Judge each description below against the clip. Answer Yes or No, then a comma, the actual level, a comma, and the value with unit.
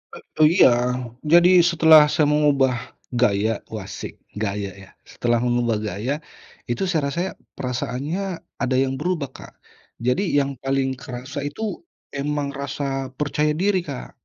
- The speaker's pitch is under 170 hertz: Yes, low, 135 Hz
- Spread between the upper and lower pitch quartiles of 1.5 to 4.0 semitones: Yes, average, 3.6 semitones